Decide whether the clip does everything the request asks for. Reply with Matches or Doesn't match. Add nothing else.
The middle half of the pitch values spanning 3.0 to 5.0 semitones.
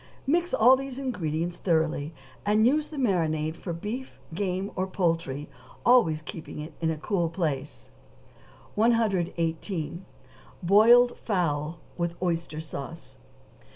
Doesn't match